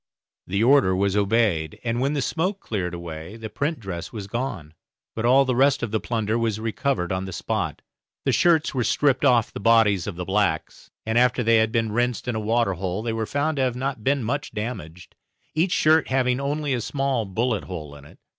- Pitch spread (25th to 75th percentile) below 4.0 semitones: No, average, 5.1 semitones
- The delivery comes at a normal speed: No, fast, 215 wpm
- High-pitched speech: No, low, 115 Hz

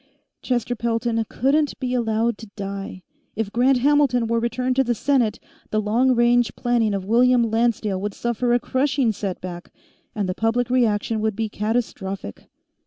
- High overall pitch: Yes, high, 230 Hz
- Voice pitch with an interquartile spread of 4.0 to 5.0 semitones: No, narrow, 2.6 semitones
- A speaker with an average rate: Yes, average, 160 wpm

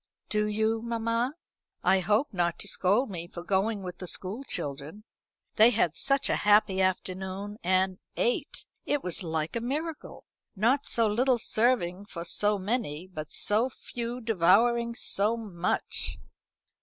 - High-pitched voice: Yes, high, 210 Hz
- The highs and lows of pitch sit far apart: No, average, 4.1 semitones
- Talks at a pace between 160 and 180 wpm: No, average, 145 wpm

